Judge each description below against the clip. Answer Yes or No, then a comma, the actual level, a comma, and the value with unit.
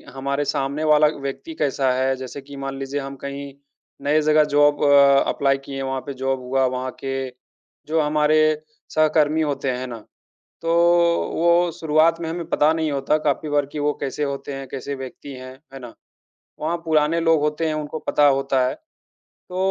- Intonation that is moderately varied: No, narrow, 2.2 semitones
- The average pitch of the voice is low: No, medium, 145 Hz